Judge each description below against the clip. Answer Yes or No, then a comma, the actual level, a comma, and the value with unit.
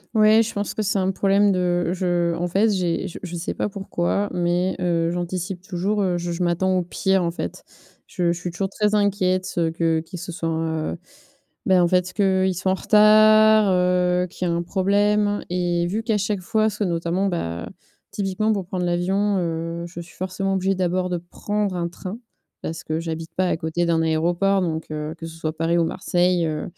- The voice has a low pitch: No, medium, 180 Hz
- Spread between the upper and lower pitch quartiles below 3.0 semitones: Yes, narrow, 2.4 semitones